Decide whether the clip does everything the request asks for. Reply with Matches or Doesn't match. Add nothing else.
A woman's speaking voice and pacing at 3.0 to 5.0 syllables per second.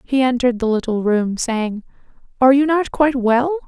Doesn't match